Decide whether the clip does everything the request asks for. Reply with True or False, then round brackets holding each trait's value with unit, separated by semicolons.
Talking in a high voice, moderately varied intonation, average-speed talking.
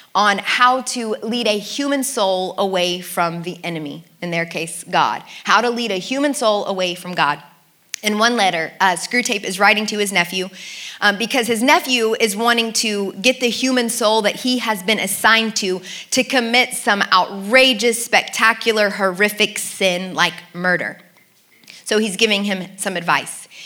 True (210 Hz; 4.0 semitones; 165 wpm)